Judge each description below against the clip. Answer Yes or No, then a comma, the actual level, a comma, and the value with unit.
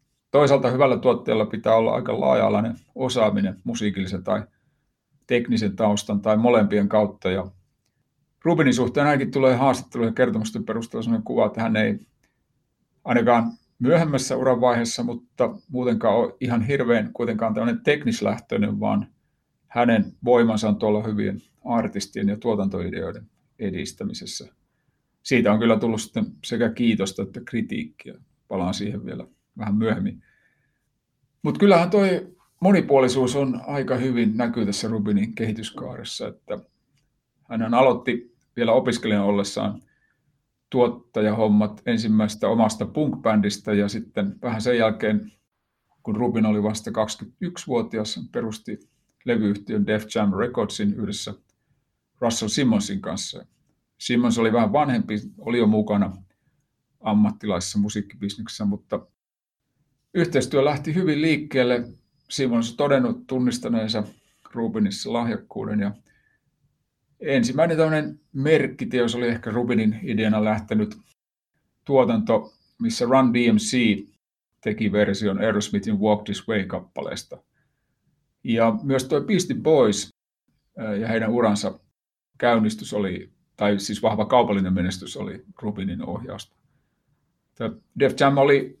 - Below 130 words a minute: Yes, average, 110 wpm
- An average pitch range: Yes, average, 4.0 semitones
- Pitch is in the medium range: No, low, 115 Hz